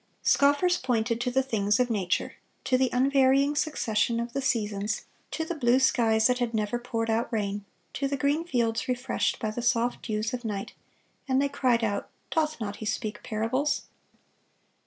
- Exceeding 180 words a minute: No, average, 170 wpm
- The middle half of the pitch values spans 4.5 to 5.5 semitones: No, average, 3.3 semitones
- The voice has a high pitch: Yes, high, 240 Hz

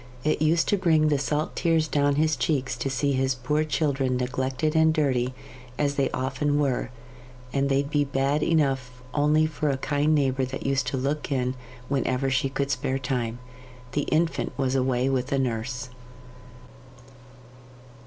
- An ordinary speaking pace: Yes, average, 165 wpm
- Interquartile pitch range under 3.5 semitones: Yes, narrow, 2.5 semitones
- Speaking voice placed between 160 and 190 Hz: No, low, 135 Hz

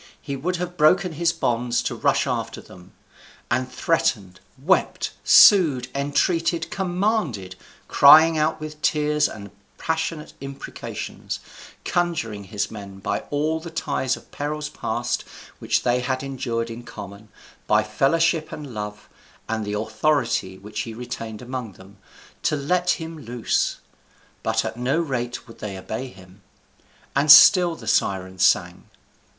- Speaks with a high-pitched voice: No, low, 130 Hz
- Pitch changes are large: Yes, wide, 6.6 semitones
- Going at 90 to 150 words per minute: Yes, average, 140 wpm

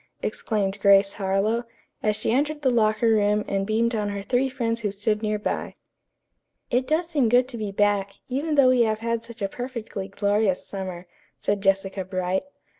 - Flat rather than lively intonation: No, average, 3.2 semitones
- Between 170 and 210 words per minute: Yes, average, 185 wpm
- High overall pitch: Yes, high, 215 Hz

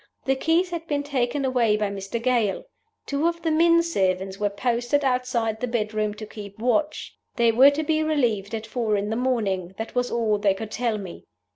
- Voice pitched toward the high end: Yes, high, 235 Hz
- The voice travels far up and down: No, average, 5.0 semitones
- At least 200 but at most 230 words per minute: Yes, fast, 205 wpm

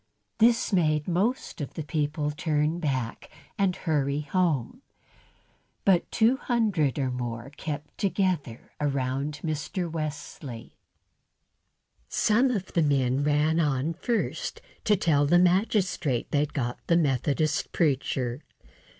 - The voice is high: No, medium, 150 Hz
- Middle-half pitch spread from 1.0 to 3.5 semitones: No, average, 4.3 semitones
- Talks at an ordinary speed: No, slow, 115 wpm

